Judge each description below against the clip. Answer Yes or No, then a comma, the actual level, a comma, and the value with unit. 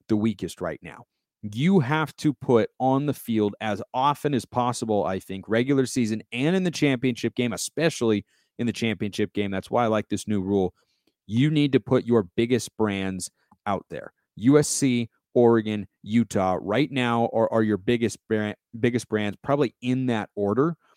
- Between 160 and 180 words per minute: Yes, average, 170 wpm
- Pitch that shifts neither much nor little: Yes, average, 3.9 semitones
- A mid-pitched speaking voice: No, low, 115 Hz